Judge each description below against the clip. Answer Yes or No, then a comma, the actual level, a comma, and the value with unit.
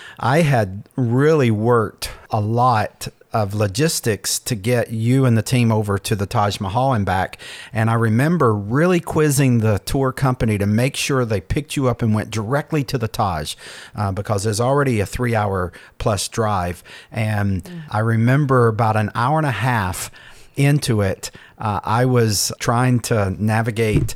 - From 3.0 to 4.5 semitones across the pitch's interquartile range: Yes, average, 3.5 semitones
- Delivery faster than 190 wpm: No, average, 170 wpm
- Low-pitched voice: Yes, low, 115 Hz